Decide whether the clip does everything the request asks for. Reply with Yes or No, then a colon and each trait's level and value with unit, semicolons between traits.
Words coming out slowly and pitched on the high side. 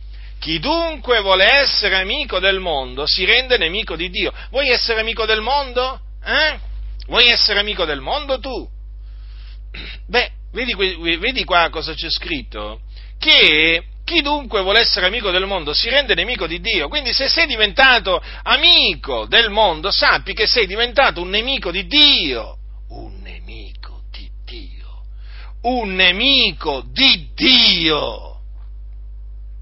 No: average, 135 wpm; high, 195 Hz